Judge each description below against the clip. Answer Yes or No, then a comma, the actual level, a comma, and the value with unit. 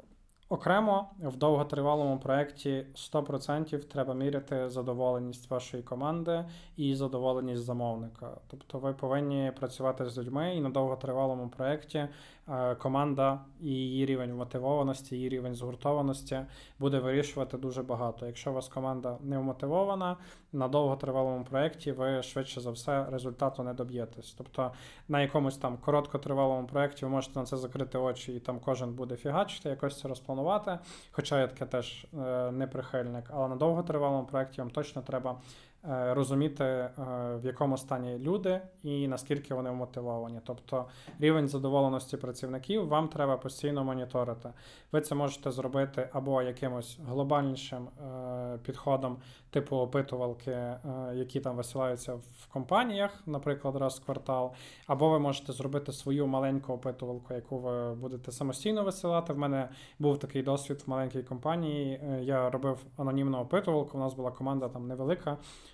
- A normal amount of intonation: No, narrow, 2.0 semitones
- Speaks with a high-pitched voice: No, low, 135 Hz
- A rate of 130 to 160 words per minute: Yes, average, 135 wpm